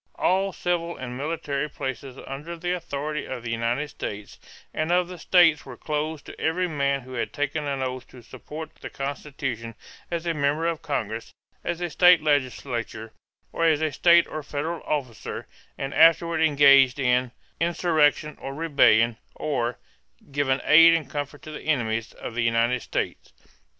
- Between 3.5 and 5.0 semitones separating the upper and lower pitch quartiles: Yes, average, 4.0 semitones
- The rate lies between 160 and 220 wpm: Yes, average, 165 wpm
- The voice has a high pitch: No, medium, 145 Hz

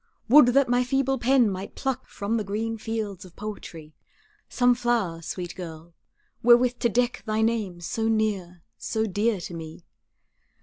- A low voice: No, high, 220 Hz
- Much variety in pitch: No, average, 4.7 semitones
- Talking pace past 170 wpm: No, average, 160 wpm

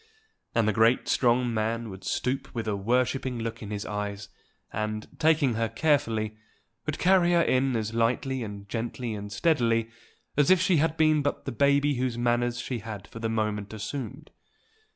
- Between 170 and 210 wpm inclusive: Yes, average, 175 wpm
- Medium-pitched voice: No, low, 115 Hz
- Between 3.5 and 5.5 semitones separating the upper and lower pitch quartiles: Yes, average, 3.9 semitones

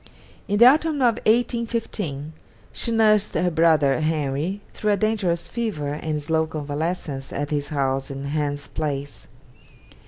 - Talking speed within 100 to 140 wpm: Yes, slow, 135 wpm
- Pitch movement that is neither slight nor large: No, wide, 6.7 semitones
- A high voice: No, medium, 160 Hz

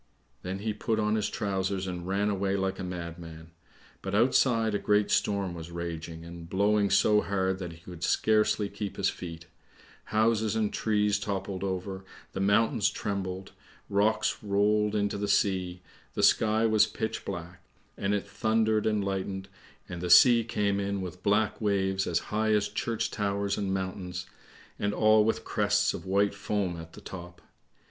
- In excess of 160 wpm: Yes, average, 170 wpm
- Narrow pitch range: Yes, narrow, 2.2 semitones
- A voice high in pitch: No, low, 100 Hz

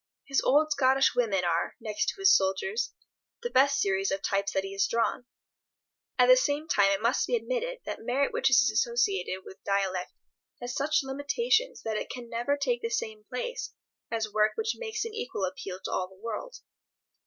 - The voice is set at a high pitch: Yes, high, 245 Hz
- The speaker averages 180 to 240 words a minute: Yes, average, 190 wpm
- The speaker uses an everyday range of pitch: No, wide, 7.3 semitones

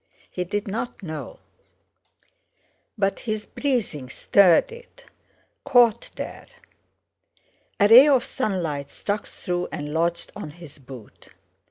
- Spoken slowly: Yes, slow, 115 wpm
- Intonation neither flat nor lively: No, wide, 6.6 semitones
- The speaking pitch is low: No, high, 195 Hz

